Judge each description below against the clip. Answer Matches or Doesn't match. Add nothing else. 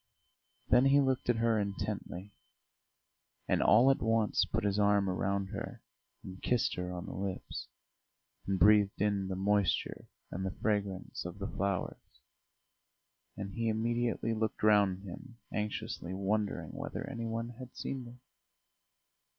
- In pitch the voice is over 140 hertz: Doesn't match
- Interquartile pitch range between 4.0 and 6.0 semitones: Doesn't match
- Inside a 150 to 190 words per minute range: Doesn't match